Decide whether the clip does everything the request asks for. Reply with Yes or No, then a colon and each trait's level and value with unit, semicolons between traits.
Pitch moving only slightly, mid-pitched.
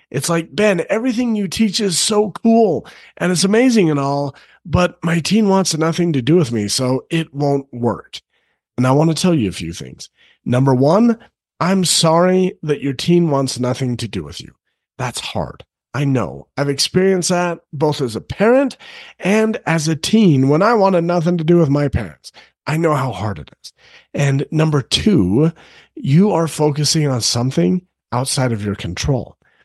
No: average, 5.3 semitones; medium, 160 Hz